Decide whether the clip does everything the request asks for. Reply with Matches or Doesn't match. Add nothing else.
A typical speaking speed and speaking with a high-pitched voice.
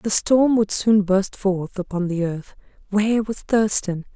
Matches